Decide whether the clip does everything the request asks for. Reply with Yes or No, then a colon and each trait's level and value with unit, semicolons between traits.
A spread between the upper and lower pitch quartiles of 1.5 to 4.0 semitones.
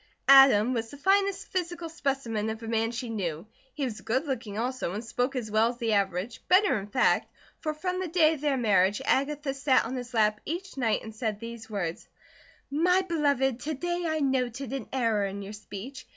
No: average, 5.2 semitones